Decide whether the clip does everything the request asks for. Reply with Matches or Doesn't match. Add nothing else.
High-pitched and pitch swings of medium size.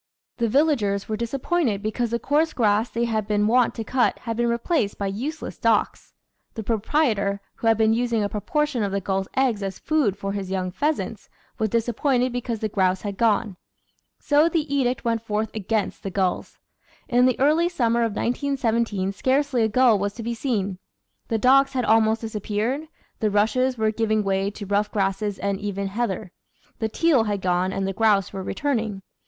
Matches